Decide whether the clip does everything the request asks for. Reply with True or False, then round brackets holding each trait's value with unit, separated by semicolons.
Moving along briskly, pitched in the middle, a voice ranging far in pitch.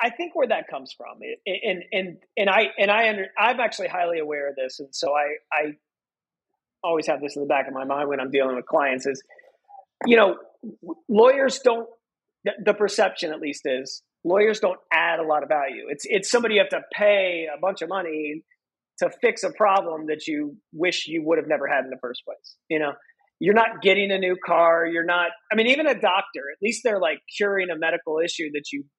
True (220 wpm; 180 Hz; 6.3 semitones)